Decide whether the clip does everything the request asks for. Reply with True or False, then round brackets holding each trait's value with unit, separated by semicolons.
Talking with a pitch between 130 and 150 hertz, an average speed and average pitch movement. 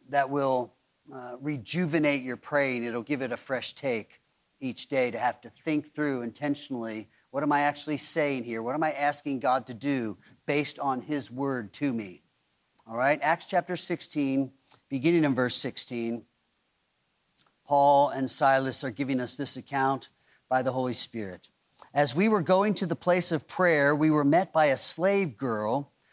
True (140 Hz; 175 wpm; 3.1 semitones)